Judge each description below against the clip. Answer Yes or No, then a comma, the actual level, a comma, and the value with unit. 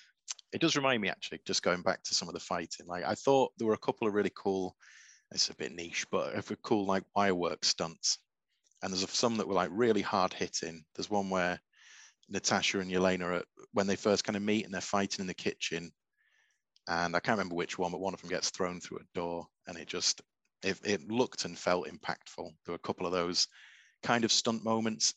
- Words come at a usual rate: No, fast, 225 wpm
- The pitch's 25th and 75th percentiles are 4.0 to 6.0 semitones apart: No, average, 3.2 semitones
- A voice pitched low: Yes, very low, 95 Hz